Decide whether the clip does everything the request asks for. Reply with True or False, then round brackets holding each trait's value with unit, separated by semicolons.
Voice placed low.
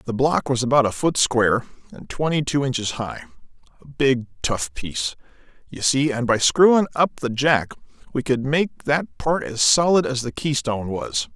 True (130 Hz)